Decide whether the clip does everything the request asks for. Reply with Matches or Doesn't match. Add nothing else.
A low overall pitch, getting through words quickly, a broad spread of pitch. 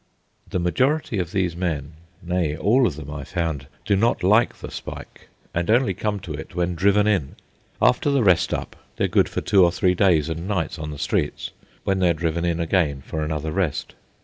Doesn't match